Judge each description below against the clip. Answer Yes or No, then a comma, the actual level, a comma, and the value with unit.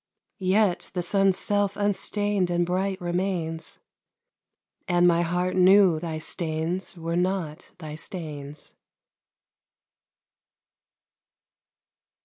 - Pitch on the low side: No, medium, 180 Hz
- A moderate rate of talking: No, slow, 90 wpm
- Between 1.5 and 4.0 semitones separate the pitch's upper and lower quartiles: Yes, average, 2.7 semitones